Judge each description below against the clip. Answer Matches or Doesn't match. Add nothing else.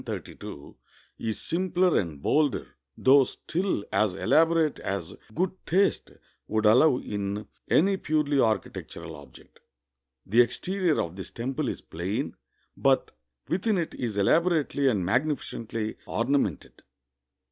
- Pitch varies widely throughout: Matches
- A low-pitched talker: Matches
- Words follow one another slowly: Matches